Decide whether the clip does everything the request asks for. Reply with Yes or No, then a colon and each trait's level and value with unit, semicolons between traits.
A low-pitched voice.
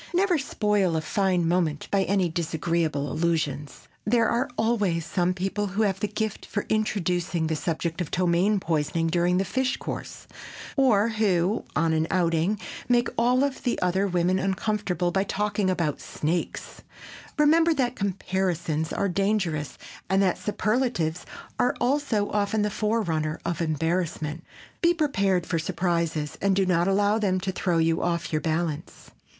No: medium, 185 Hz